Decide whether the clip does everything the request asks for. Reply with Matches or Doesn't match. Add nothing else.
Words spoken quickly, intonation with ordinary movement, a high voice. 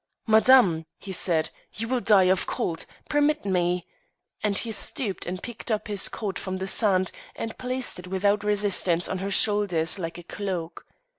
Doesn't match